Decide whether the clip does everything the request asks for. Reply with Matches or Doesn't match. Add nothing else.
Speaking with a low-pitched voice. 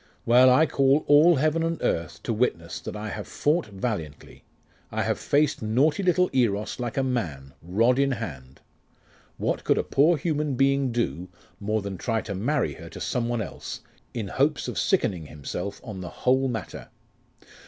Matches